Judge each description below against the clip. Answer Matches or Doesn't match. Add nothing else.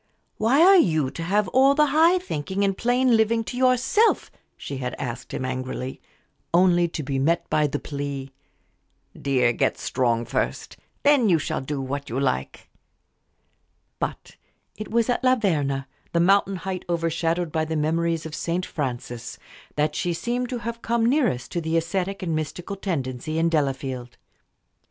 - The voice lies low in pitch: Doesn't match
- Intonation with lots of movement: Matches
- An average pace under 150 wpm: Doesn't match